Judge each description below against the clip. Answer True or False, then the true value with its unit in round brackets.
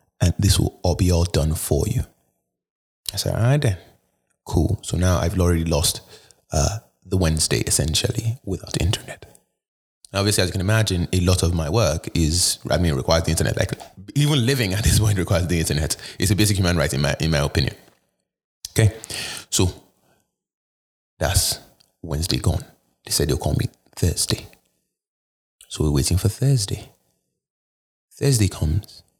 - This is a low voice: True (90 Hz)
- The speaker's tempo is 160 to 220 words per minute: True (165 wpm)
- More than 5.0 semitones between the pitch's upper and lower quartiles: True (5.4 semitones)